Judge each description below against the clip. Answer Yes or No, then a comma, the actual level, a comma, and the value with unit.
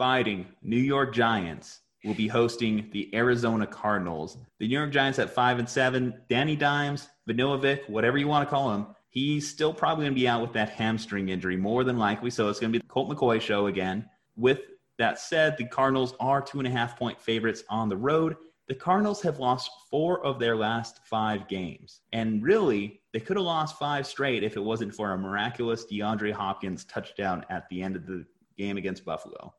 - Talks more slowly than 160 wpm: No, average, 200 wpm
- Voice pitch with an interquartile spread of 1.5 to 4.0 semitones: No, average, 4.5 semitones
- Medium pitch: No, low, 115 Hz